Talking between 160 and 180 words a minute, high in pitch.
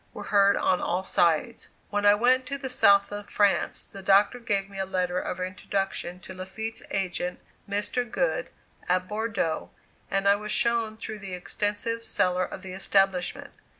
Yes: average, 170 wpm; high, 200 Hz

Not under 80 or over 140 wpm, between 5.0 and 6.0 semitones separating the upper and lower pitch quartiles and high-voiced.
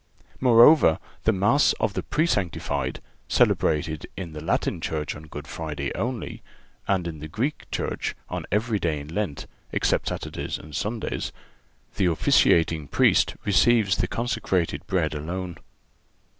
No: slow, 135 wpm; wide, 5.6 semitones; very low, 90 Hz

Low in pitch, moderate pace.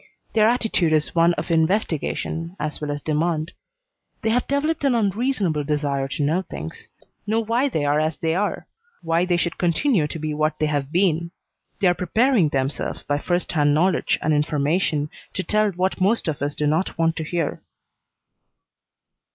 No: medium, 165 Hz; average, 175 wpm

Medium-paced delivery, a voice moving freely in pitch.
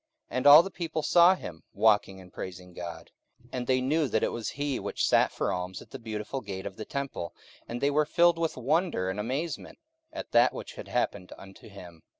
No: fast, 220 wpm; wide, 7.5 semitones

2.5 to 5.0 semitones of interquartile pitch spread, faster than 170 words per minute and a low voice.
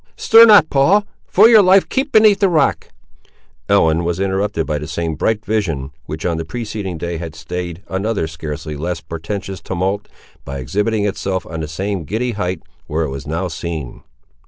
No: wide, 5.4 semitones; average, 180 wpm; very low, 90 Hz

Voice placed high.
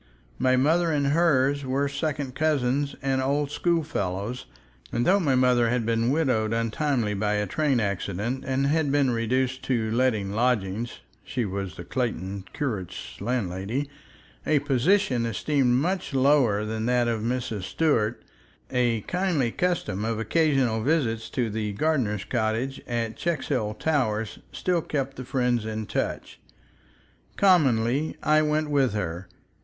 No: low, 125 Hz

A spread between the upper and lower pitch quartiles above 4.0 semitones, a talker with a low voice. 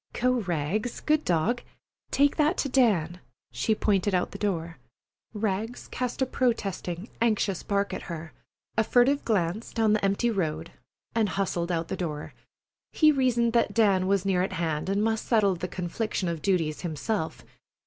No: average, 4.9 semitones; high, 200 Hz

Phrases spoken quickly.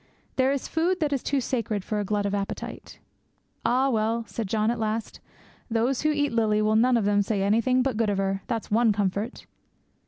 Yes: fast, 210 wpm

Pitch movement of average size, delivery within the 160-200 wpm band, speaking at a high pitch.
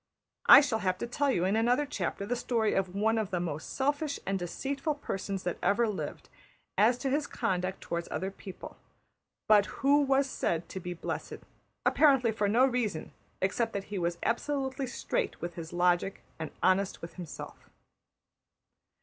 No: wide, 6.4 semitones; average, 170 wpm; high, 210 Hz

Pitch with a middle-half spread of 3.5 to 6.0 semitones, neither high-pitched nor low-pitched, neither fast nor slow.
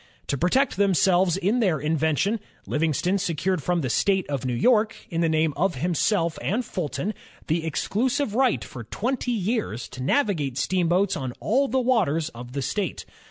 Yes: wide, 5.6 semitones; medium, 180 Hz; average, 165 wpm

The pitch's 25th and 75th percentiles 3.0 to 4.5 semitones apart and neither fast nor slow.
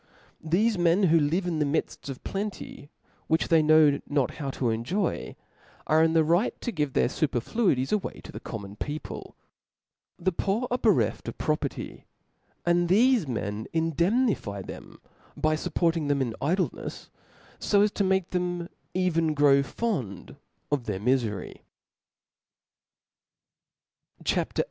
No: average, 5.0 semitones; average, 145 wpm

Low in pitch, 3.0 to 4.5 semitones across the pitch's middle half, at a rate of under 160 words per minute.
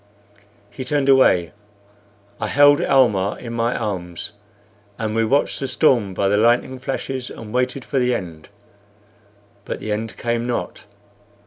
Yes: low, 115 Hz; average, 4.1 semitones; average, 145 wpm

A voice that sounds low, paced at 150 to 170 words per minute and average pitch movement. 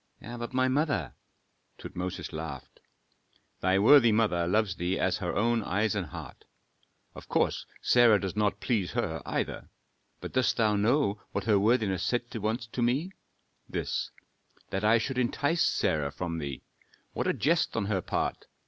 Yes: low, 105 Hz; average, 155 wpm; average, 4.4 semitones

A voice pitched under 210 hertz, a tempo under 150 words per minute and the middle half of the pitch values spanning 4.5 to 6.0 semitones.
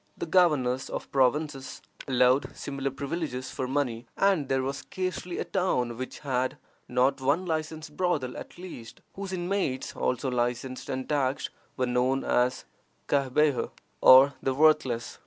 No: low, 135 Hz; average, 140 wpm; average, 3.5 semitones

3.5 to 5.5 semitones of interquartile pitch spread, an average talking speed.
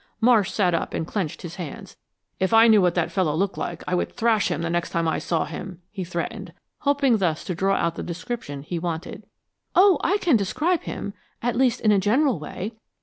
No: average, 5.2 semitones; fast, 215 wpm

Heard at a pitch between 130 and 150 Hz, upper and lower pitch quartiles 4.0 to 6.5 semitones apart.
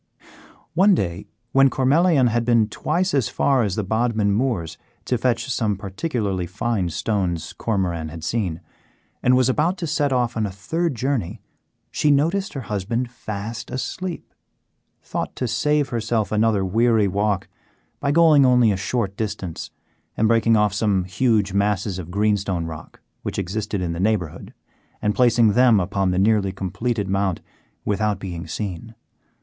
No: low, 110 Hz; average, 4.4 semitones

